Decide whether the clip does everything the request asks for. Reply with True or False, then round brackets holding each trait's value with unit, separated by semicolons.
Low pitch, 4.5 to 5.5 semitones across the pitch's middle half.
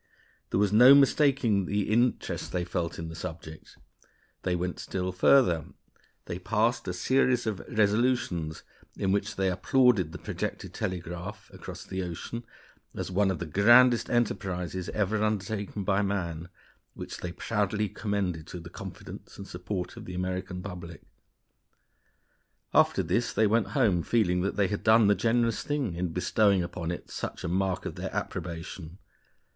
False (95 Hz; 3.6 semitones)